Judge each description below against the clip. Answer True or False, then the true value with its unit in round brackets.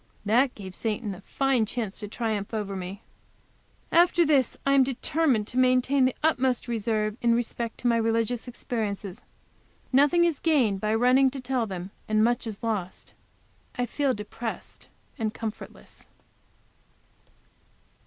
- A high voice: True (235 Hz)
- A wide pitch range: False (3.5 semitones)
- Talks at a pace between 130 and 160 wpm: True (145 wpm)